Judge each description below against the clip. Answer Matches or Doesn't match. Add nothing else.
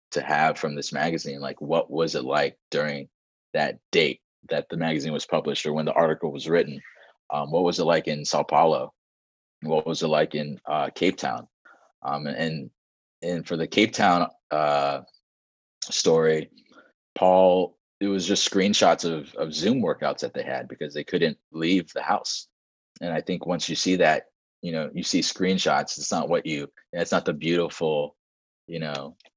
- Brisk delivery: Doesn't match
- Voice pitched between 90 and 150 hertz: Doesn't match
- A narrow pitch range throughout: Doesn't match